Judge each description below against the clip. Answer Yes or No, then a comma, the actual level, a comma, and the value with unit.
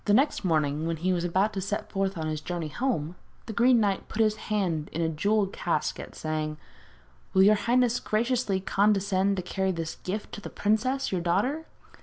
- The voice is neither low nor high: No, high, 195 Hz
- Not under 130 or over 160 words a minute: No, average, 190 wpm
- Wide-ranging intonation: No, average, 4.2 semitones